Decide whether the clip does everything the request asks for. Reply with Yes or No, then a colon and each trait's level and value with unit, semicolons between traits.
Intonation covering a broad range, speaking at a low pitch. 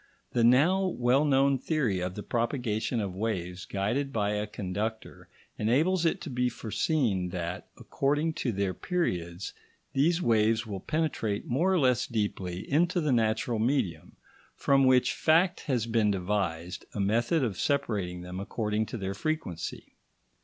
Yes: wide, 5.9 semitones; low, 115 Hz